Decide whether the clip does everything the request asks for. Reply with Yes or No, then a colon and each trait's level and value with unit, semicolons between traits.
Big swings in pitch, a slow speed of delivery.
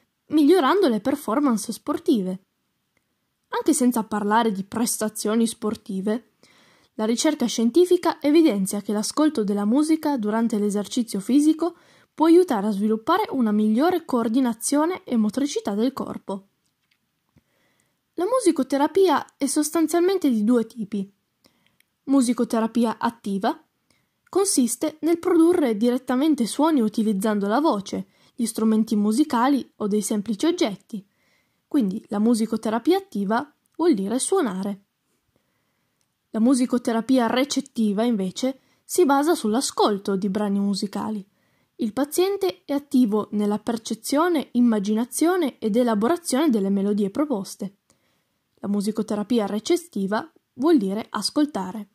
Yes: wide, 5.7 semitones; slow, 105 wpm